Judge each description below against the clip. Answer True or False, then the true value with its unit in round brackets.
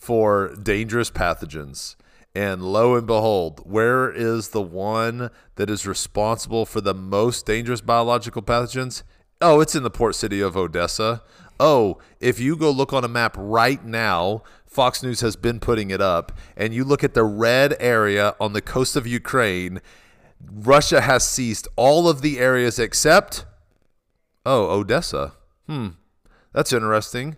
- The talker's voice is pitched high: False (115 Hz)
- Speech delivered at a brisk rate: False (155 wpm)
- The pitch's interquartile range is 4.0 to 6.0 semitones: False (3.3 semitones)